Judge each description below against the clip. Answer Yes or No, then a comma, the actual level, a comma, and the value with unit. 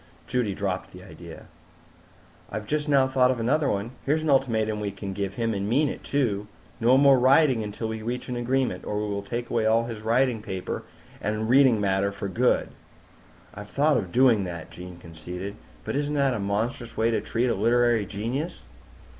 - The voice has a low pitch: Yes, low, 115 Hz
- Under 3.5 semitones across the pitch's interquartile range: No, average, 4.3 semitones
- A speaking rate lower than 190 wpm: No, average, 195 wpm